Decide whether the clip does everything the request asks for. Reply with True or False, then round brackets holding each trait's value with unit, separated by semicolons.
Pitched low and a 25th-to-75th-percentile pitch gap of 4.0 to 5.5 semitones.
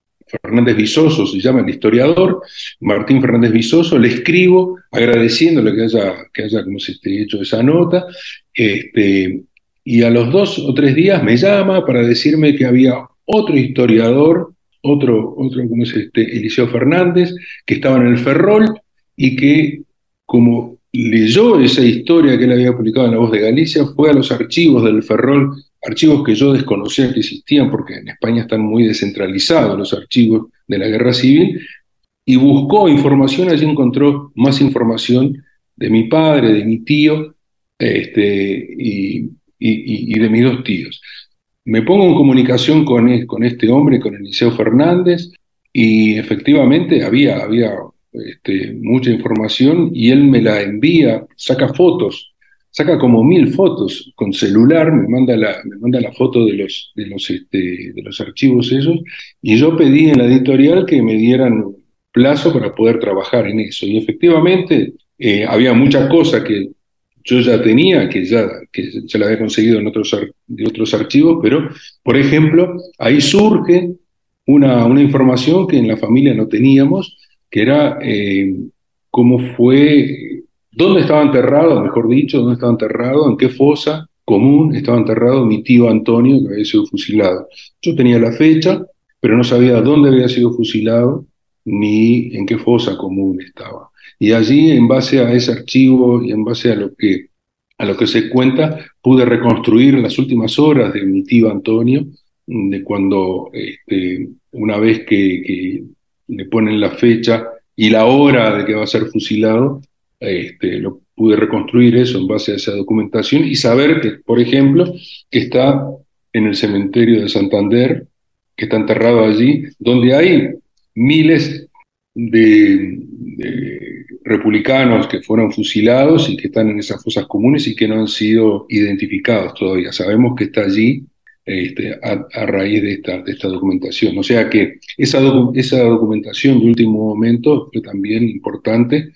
True (125 Hz; 4.4 semitones)